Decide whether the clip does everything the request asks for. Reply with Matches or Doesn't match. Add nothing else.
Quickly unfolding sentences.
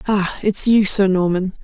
Doesn't match